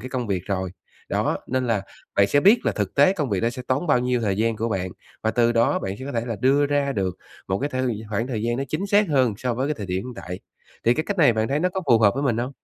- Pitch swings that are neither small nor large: Yes, average, 4.5 semitones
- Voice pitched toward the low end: Yes, low, 120 Hz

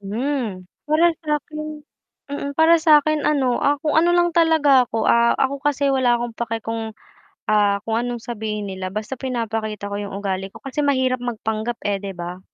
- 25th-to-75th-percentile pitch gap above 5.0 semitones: Yes, wide, 5.4 semitones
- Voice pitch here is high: Yes, high, 240 Hz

